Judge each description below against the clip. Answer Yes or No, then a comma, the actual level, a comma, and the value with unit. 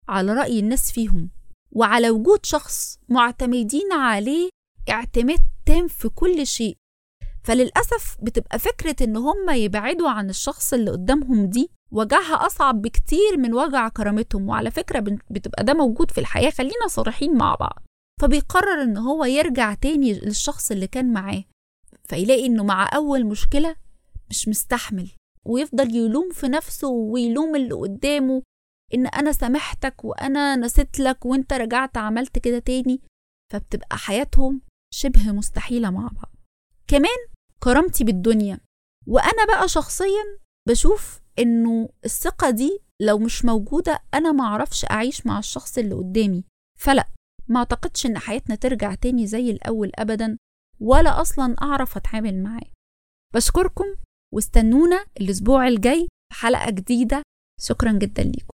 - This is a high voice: Yes, very high, 255 Hz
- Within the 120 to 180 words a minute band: Yes, average, 130 wpm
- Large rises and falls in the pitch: No, average, 4.5 semitones